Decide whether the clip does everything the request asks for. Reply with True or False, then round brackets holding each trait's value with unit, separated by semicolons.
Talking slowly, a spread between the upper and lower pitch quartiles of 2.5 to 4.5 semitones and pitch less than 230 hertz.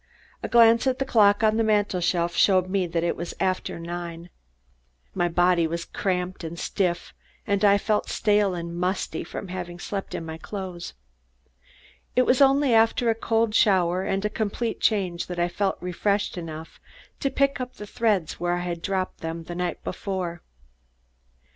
False (175 wpm; 3.5 semitones; 185 Hz)